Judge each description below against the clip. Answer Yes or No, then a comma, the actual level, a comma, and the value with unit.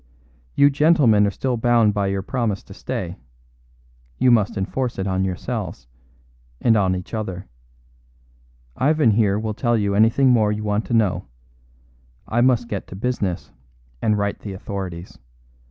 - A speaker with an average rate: Yes, average, 155 wpm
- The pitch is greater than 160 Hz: No, low, 105 Hz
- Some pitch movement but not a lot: Yes, average, 3.4 semitones